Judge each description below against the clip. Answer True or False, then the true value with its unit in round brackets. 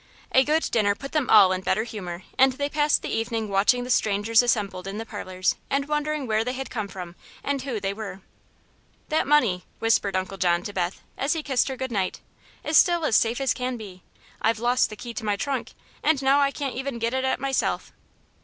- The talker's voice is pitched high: True (230 Hz)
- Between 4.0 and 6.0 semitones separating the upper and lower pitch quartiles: True (5.2 semitones)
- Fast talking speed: True (225 wpm)